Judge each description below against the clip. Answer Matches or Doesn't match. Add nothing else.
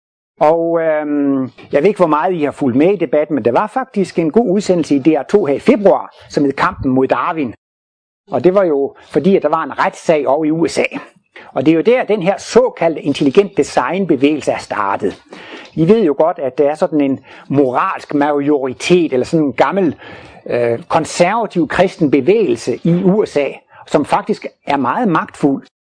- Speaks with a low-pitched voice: Doesn't match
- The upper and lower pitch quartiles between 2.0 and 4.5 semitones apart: Doesn't match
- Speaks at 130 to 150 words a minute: Doesn't match